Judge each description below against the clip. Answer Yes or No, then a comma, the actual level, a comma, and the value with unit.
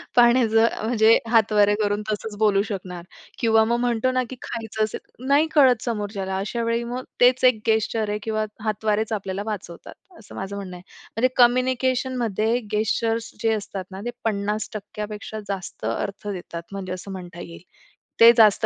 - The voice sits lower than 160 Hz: No, high, 215 Hz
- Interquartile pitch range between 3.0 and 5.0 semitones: No, narrow, 2.6 semitones